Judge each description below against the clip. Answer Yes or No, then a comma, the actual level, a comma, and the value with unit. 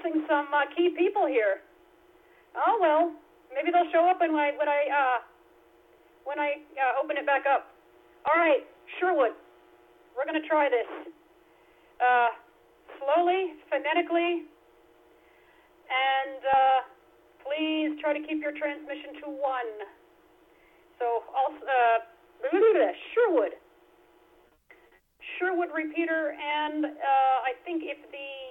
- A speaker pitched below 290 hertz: No, very high, 295 Hz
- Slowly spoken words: Yes, slow, 120 wpm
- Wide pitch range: No, average, 3.7 semitones